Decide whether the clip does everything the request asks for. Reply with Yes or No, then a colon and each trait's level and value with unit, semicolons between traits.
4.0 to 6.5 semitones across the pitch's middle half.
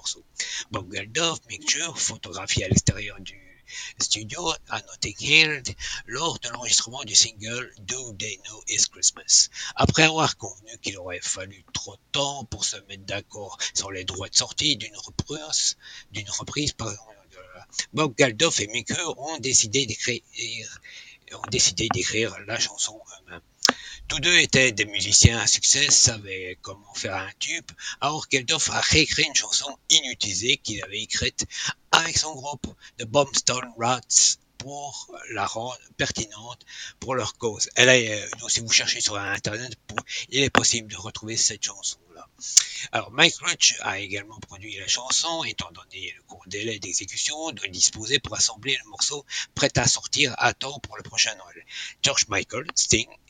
Yes: average, 5.0 semitones